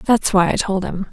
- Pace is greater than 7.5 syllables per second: No, 5.7 syllables/s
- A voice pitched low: No, high, 195 Hz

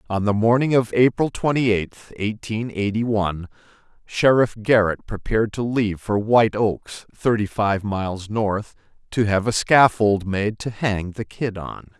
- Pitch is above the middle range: No, low, 105 Hz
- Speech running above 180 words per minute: No, average, 160 wpm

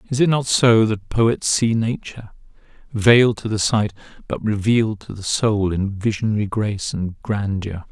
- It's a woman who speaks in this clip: No, male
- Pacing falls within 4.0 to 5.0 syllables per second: Yes, 4.7 syllables/s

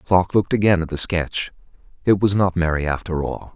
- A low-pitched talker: Yes, very low, 90 Hz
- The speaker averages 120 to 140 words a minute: No, fast, 205 wpm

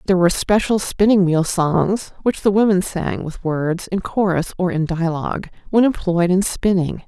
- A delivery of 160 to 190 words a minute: Yes, average, 180 wpm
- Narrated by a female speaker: Yes, female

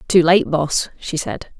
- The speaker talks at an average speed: Yes, average, 190 wpm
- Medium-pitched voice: Yes, medium, 160 Hz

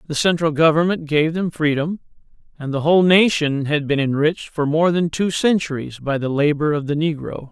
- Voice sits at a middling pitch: Yes, medium, 155 Hz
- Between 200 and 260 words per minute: No, average, 190 wpm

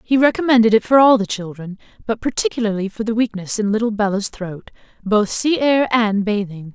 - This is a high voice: Yes, high, 220 Hz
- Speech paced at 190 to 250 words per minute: No, average, 180 wpm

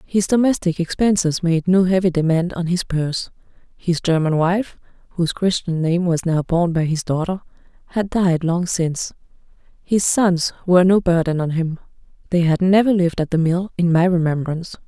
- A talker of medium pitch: Yes, medium, 175 Hz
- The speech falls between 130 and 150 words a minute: No, average, 175 wpm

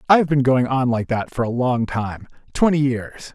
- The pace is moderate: No, fast, 215 wpm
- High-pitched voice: No, low, 130 Hz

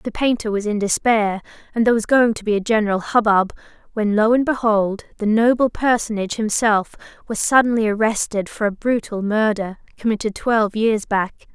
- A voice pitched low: No, high, 215 Hz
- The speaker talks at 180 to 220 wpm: No, average, 170 wpm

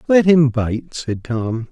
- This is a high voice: No, low, 135 Hz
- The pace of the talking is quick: No, average, 175 wpm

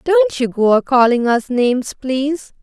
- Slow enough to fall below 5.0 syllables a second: Yes, 4.5 syllables/s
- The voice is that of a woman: Yes, female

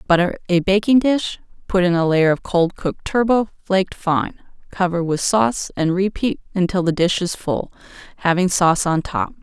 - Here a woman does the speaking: Yes, female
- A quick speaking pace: No, average, 180 wpm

